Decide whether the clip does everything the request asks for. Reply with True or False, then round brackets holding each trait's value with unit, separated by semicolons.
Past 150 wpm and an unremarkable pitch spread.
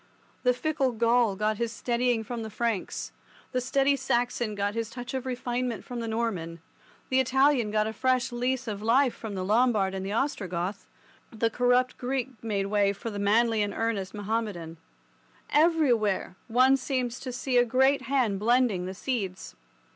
True (170 wpm; 3.4 semitones)